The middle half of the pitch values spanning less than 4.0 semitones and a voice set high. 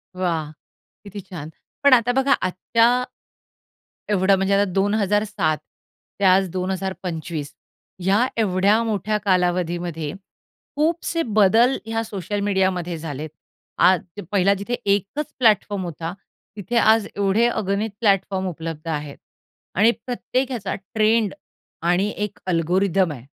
Yes: average, 3.4 semitones; high, 195 Hz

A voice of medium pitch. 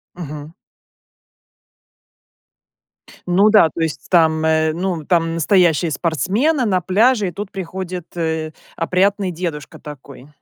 Yes: medium, 175 Hz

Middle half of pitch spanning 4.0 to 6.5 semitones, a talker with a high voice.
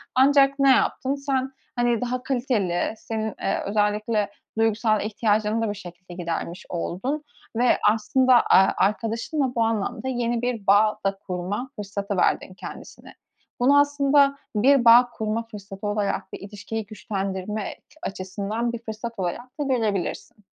No: average, 3.6 semitones; high, 220 Hz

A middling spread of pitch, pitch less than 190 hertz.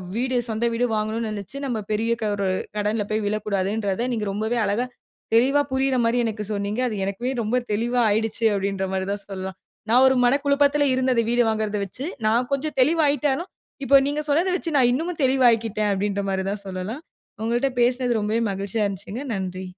No: average, 4.1 semitones; high, 230 Hz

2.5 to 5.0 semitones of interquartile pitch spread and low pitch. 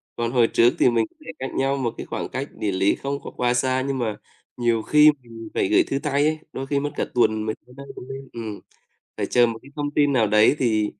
Yes: average, 3.5 semitones; low, 125 Hz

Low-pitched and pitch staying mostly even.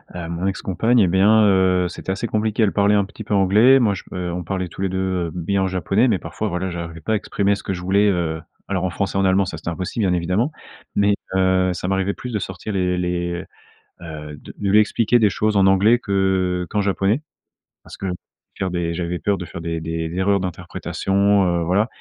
Yes: very low, 95 Hz; narrow, 2.3 semitones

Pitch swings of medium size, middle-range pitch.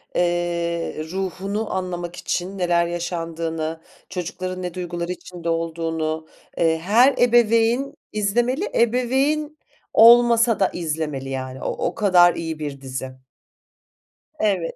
Yes: average, 4.9 semitones; medium, 175 Hz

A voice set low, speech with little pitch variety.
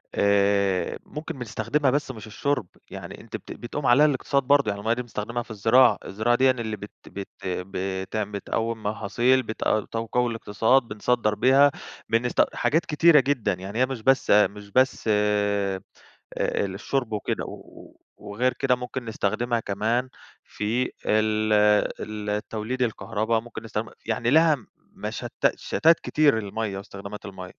No: low, 115 Hz; average, 3.6 semitones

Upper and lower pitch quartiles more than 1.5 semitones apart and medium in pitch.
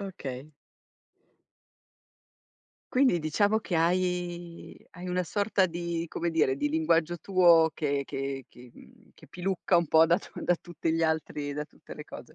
Yes: narrow, 2.5 semitones; medium, 170 Hz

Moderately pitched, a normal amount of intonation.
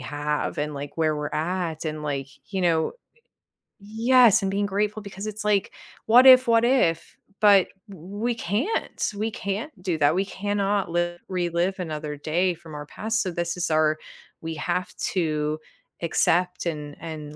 Yes: medium, 180 Hz; average, 4.7 semitones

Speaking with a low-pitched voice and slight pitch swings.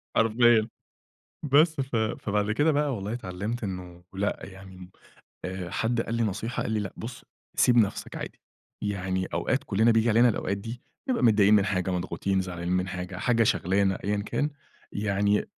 No: low, 105 Hz; average, 3.6 semitones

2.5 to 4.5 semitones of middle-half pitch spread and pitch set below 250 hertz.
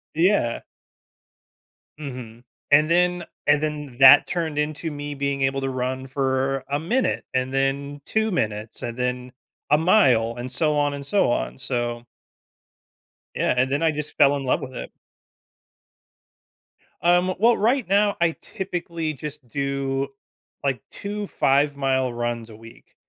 Yes: average, 3.8 semitones; medium, 140 Hz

